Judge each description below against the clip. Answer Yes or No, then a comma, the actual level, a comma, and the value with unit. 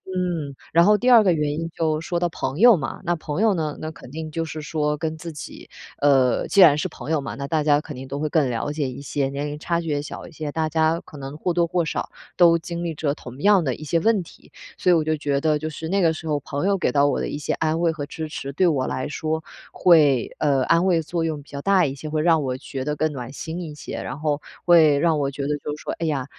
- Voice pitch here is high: No, medium, 155 Hz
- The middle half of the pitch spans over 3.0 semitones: No, narrow, 2.6 semitones